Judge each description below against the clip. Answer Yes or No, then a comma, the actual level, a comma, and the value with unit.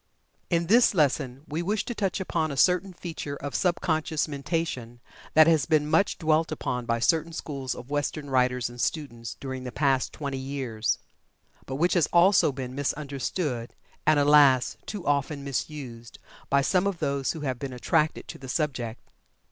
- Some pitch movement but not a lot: Yes, average, 3.8 semitones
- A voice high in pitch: No, medium, 145 Hz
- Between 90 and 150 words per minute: No, average, 170 wpm